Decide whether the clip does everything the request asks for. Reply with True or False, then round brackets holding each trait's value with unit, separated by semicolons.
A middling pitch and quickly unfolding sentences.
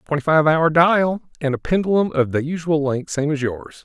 True (155 Hz; 220 wpm)